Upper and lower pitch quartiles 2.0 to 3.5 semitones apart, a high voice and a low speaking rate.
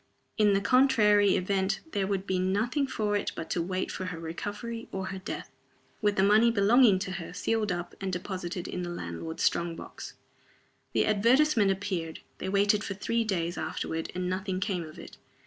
No: narrow, 2.6 semitones; high, 195 Hz; average, 180 wpm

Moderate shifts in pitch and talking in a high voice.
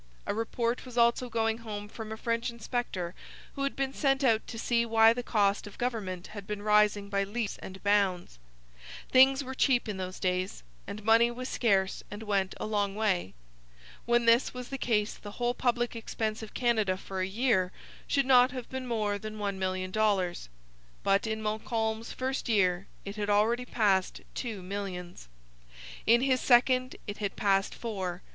Yes: average, 3.3 semitones; high, 220 Hz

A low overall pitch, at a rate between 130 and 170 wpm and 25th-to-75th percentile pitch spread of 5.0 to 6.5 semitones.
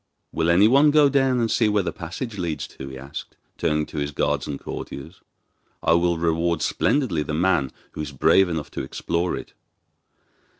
No: very low, 85 Hz; average, 180 wpm; wide, 5.6 semitones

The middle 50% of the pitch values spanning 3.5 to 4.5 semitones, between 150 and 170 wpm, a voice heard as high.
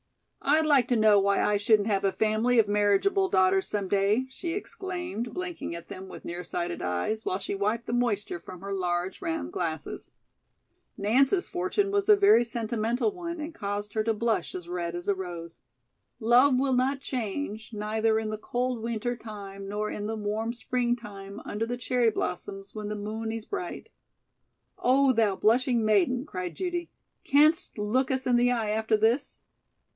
No: average, 4.1 semitones; average, 180 wpm; high, 220 Hz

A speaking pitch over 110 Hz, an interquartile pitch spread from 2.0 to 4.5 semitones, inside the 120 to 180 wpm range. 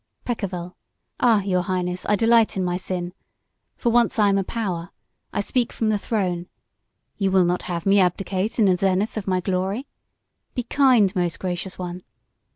Yes: high, 190 Hz; average, 3.2 semitones; average, 175 wpm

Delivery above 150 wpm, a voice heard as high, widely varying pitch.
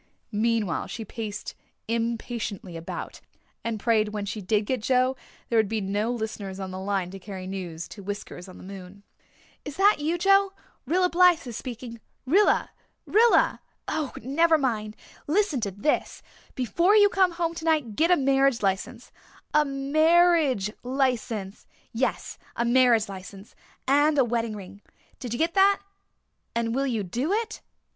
Yes: average, 160 wpm; high, 235 Hz; wide, 6.9 semitones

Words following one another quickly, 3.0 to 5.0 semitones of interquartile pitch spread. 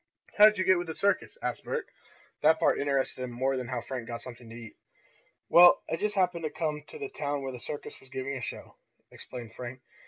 No: fast, 230 wpm; wide, 5.6 semitones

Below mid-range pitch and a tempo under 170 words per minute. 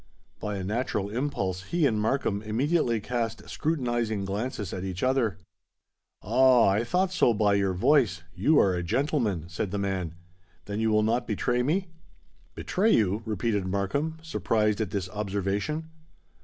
Yes: low, 110 Hz; average, 150 wpm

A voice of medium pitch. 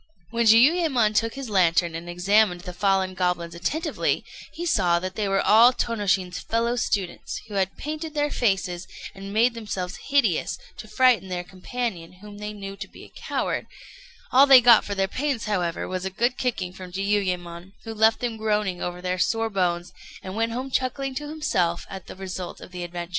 No: high, 200 Hz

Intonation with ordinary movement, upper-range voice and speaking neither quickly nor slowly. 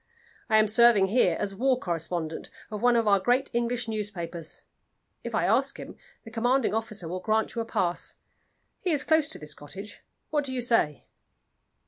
Yes: average, 4.7 semitones; high, 220 Hz; average, 180 wpm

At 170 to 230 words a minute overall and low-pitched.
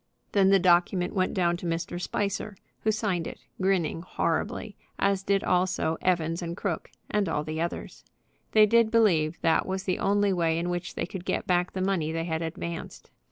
No: average, 190 wpm; medium, 180 Hz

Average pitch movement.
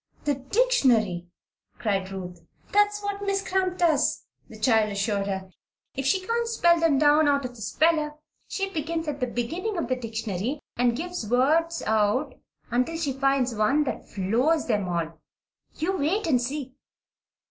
No: wide, 7.1 semitones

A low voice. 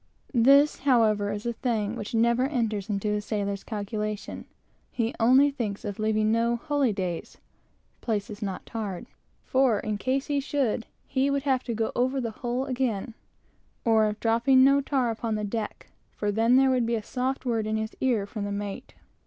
No: high, 230 Hz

